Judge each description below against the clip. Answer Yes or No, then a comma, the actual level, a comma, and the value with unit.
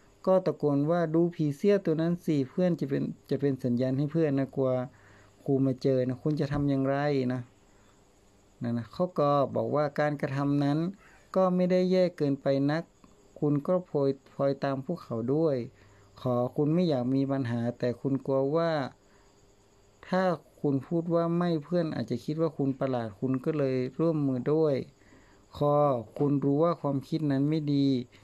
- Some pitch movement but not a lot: Yes, average, 3.8 semitones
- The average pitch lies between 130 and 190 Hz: Yes, medium, 140 Hz